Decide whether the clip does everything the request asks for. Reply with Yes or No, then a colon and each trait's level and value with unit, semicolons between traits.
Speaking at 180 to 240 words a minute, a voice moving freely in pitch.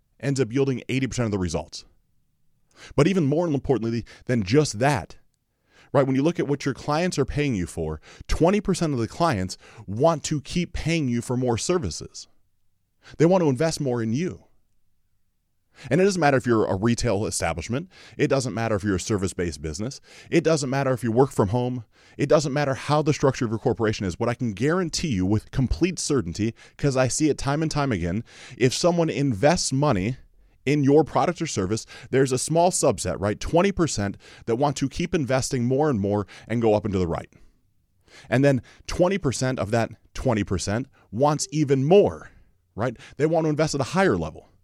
Yes: average, 190 wpm; wide, 5.9 semitones